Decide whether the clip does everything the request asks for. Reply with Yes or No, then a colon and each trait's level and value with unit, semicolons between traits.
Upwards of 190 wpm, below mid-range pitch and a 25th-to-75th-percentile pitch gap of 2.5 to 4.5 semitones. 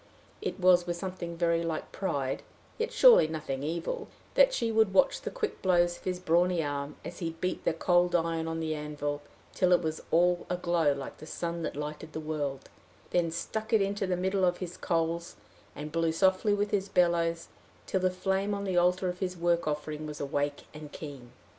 No: average, 200 wpm; medium, 170 Hz; average, 2.9 semitones